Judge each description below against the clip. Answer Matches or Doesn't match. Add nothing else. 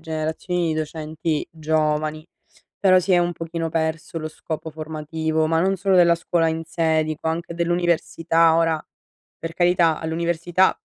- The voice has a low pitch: Doesn't match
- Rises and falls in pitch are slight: Matches